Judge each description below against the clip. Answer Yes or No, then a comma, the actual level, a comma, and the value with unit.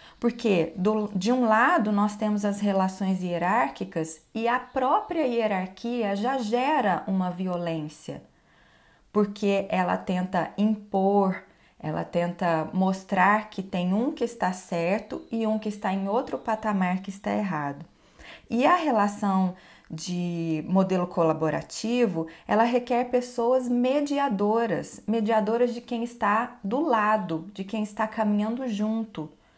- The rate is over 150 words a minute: No, average, 125 wpm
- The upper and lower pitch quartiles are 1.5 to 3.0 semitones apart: No, average, 4.0 semitones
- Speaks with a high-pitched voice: Yes, high, 205 Hz